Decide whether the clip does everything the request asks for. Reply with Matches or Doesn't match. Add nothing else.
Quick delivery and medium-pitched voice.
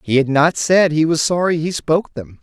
Matches